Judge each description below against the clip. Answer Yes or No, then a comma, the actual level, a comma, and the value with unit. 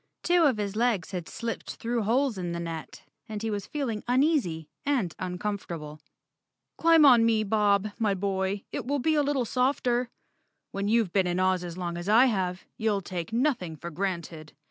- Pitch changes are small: No, average, 5.3 semitones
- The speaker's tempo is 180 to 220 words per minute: Yes, average, 190 wpm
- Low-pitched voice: No, high, 205 Hz